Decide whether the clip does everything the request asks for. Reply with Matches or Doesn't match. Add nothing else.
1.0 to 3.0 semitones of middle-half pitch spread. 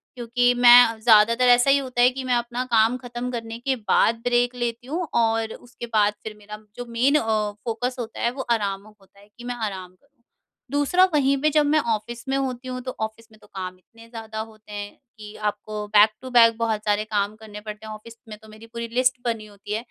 Matches